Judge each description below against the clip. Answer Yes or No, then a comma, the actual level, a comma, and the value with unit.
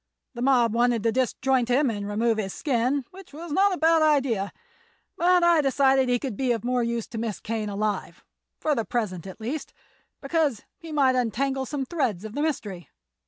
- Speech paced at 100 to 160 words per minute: No, average, 185 wpm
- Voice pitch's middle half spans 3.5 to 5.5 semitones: Yes, average, 4.3 semitones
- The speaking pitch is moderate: No, very high, 250 Hz